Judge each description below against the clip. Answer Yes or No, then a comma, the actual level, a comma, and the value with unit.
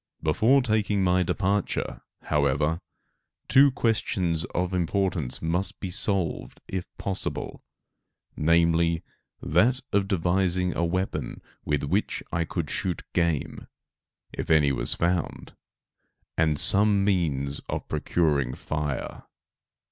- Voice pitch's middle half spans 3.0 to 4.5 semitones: Yes, average, 4.1 semitones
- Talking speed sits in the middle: No, slow, 110 wpm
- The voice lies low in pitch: Yes, very low, 85 Hz